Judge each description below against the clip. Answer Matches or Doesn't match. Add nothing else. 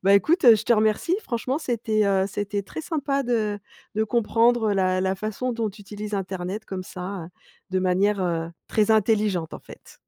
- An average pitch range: Matches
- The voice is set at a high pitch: Matches